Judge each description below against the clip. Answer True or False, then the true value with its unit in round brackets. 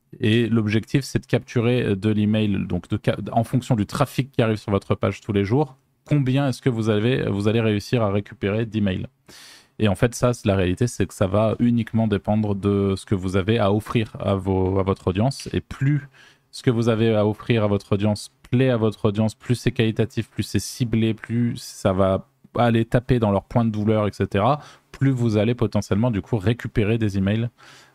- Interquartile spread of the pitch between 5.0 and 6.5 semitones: False (3.2 semitones)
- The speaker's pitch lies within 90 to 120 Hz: True (110 Hz)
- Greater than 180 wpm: True (215 wpm)